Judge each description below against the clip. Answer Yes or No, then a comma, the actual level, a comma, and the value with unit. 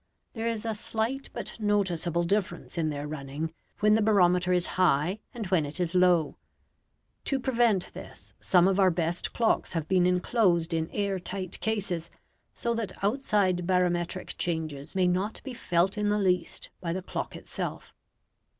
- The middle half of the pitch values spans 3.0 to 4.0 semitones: Yes, average, 3.5 semitones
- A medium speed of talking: Yes, average, 165 wpm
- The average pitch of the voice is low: No, medium, 185 Hz